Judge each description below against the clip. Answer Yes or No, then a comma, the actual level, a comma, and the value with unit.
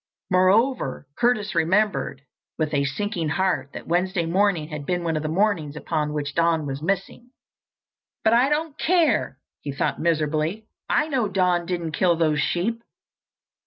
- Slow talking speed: No, average, 155 wpm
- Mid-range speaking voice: Yes, medium, 175 Hz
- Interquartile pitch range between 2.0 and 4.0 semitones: No, average, 5.2 semitones